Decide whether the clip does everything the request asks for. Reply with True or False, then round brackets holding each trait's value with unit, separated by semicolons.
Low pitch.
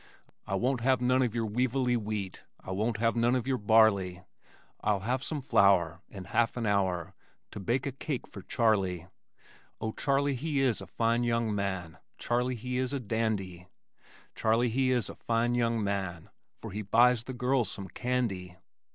True (115 Hz)